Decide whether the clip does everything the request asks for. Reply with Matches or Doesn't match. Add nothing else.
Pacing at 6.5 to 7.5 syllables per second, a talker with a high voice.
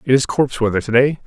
Doesn't match